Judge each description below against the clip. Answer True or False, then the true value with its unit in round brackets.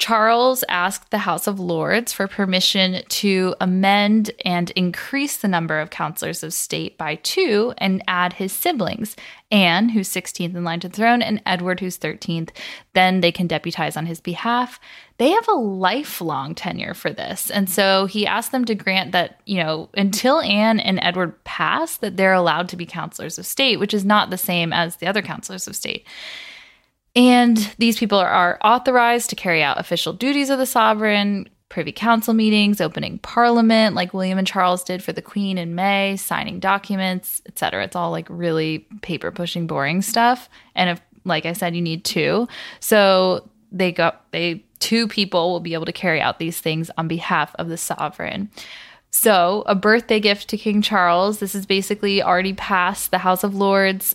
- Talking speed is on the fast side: False (185 wpm)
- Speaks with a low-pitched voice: False (190 Hz)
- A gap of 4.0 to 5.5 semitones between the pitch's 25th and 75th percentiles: False (3.5 semitones)